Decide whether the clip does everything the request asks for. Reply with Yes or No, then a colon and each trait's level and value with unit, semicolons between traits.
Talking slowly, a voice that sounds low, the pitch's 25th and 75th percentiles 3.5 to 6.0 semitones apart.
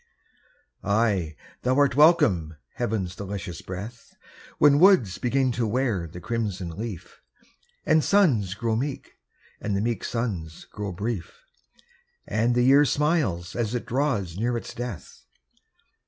Yes: slow, 130 wpm; low, 115 Hz; average, 5.3 semitones